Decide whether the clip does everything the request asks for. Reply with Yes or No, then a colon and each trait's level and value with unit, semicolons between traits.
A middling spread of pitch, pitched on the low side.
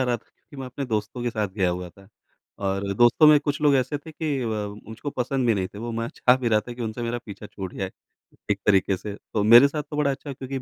Yes: average, 4.6 semitones; low, 120 Hz